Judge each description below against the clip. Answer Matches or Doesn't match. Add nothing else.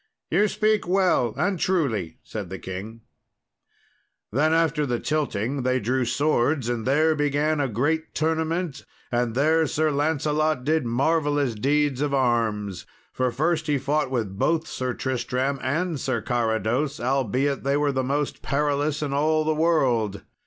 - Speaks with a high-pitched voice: Doesn't match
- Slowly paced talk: Doesn't match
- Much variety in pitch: Doesn't match